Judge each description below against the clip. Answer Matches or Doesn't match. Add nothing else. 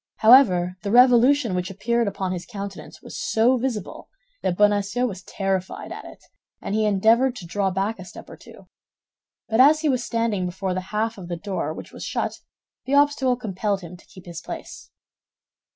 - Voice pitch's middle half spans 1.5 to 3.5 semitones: Doesn't match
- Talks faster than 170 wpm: Matches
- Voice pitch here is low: Doesn't match